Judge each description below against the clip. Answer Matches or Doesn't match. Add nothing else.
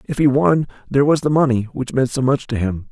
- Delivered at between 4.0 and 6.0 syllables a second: Matches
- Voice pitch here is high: Doesn't match